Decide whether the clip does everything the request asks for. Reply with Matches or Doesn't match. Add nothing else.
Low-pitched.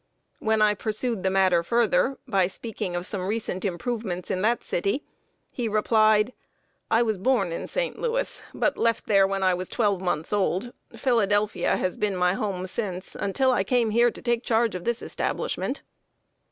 Doesn't match